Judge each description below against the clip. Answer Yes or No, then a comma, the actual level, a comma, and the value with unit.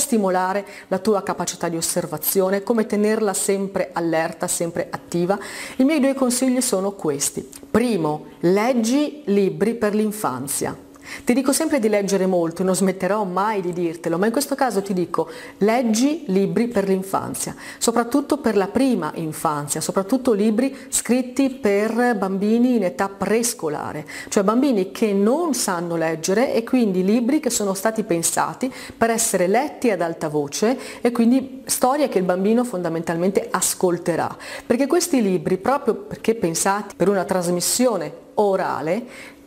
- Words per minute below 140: No, average, 145 wpm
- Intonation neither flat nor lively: Yes, average, 5.0 semitones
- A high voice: Yes, high, 205 Hz